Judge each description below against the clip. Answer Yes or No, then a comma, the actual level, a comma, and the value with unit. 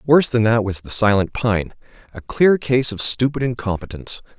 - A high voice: No, low, 115 Hz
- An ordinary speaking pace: Yes, average, 165 wpm